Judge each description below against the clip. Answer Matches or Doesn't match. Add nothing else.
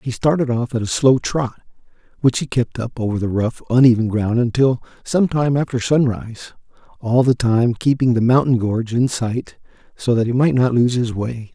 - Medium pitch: Doesn't match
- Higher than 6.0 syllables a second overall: Doesn't match